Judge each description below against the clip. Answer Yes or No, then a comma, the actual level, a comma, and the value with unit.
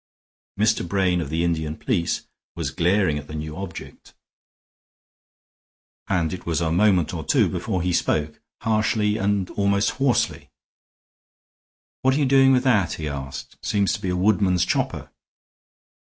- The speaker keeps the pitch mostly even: No, average, 4.4 semitones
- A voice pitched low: Yes, very low, 95 Hz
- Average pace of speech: Yes, average, 150 wpm